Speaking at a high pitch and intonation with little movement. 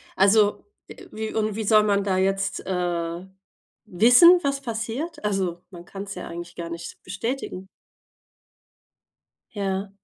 No: high, 200 Hz; average, 3.4 semitones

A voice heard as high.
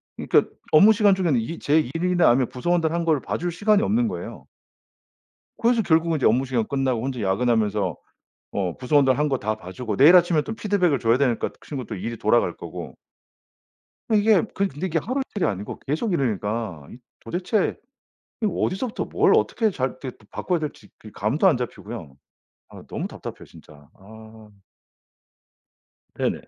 No: medium, 140 Hz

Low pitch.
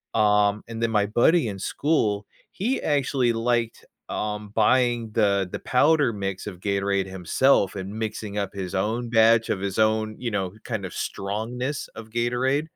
Yes: low, 110 Hz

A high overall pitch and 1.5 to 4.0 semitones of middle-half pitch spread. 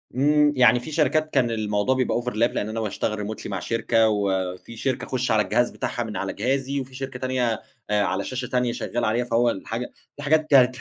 No: low, 120 Hz; average, 3.3 semitones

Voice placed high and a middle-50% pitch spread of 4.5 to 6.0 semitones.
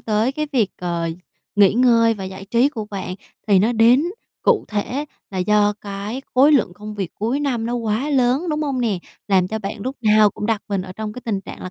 No: high, 220 Hz; average, 3.9 semitones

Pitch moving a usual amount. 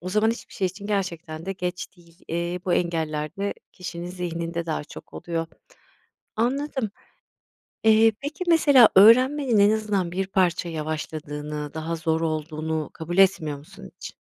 Yes: average, 4.2 semitones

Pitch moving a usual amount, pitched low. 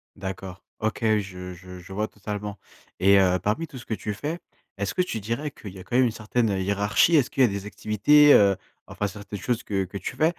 Yes: average, 3.6 semitones; low, 105 Hz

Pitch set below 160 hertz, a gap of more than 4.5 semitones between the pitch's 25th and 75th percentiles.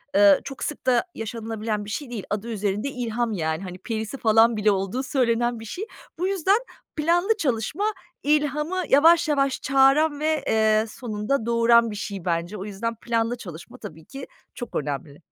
No: high, 230 Hz; average, 4.9 semitones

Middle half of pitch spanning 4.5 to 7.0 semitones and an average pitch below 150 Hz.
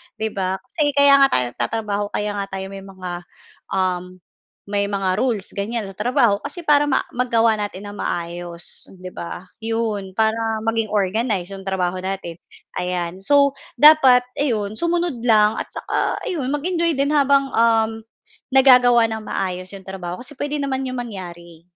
No: average, 5.2 semitones; high, 215 Hz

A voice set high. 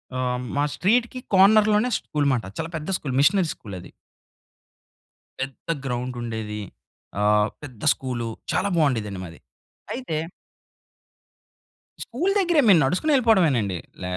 No: medium, 140 Hz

